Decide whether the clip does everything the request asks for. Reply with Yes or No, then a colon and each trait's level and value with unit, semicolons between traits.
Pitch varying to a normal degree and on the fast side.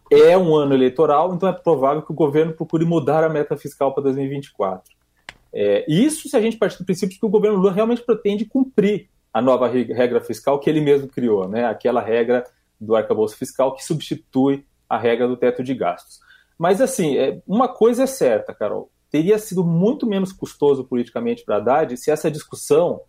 No: wide, 8.4 semitones; fast, 190 wpm